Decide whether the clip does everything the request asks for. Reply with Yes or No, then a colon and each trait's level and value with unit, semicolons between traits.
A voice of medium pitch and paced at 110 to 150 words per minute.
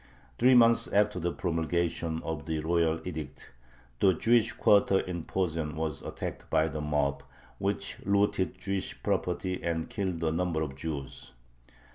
No: very low, 85 Hz; average, 145 wpm